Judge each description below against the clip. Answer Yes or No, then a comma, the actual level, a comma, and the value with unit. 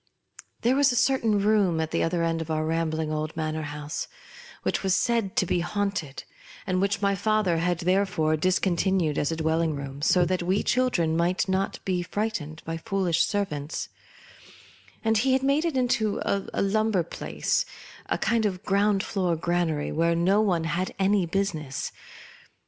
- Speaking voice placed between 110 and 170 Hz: No, medium, 180 Hz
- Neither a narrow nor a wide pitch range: Yes, average, 3.9 semitones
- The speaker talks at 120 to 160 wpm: No, average, 175 wpm